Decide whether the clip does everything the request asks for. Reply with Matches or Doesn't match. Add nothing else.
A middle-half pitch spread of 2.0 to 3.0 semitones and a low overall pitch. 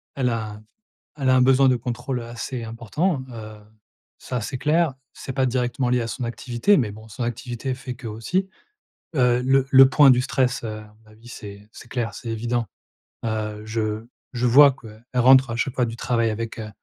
Matches